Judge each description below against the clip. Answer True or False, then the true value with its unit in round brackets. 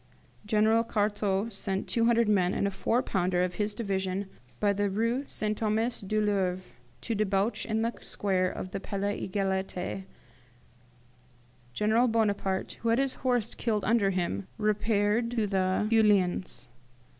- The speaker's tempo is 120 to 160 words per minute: True (145 wpm)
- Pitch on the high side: True (205 Hz)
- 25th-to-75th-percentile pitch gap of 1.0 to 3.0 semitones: True (2.7 semitones)